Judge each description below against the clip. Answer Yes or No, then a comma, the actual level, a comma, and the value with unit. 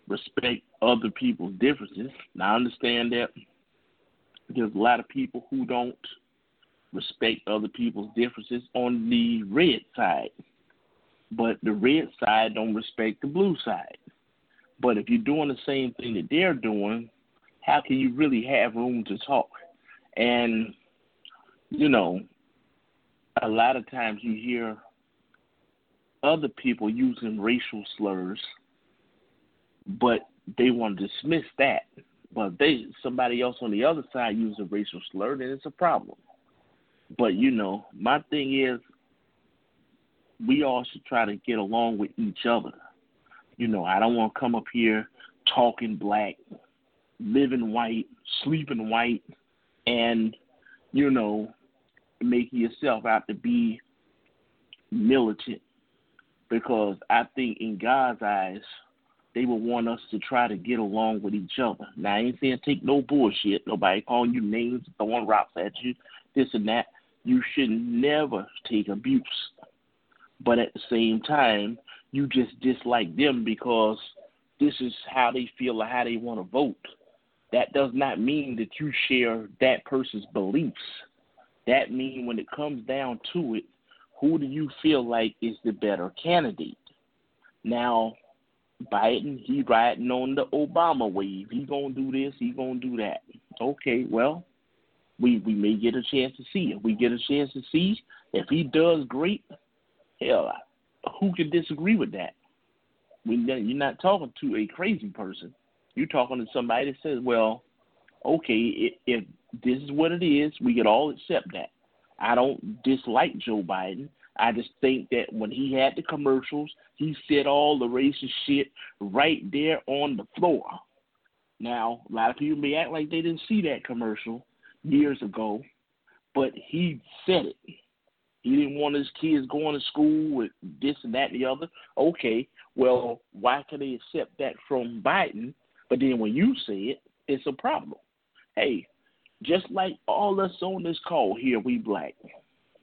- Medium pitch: No, low, 125 Hz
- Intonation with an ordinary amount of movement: Yes, average, 4.7 semitones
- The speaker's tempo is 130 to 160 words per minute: Yes, average, 155 wpm